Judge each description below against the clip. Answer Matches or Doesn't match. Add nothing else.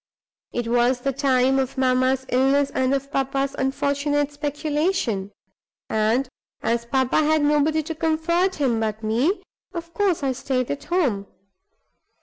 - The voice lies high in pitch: Matches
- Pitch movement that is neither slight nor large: Matches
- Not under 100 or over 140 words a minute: Matches